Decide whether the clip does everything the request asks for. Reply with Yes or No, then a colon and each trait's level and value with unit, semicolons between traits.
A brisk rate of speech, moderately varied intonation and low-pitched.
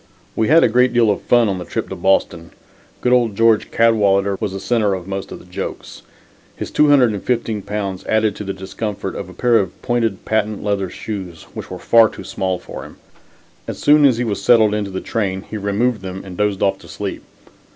Yes: fast, 215 wpm; average, 3.0 semitones; low, 105 Hz